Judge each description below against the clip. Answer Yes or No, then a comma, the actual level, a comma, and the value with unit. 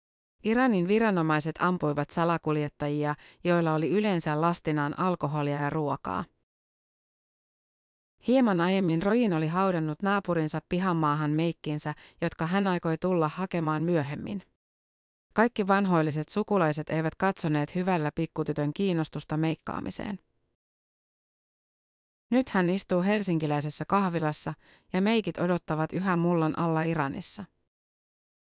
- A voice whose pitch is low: No, medium, 165 Hz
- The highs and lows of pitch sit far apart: No, average, 3.6 semitones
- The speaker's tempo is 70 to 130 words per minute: Yes, slow, 95 wpm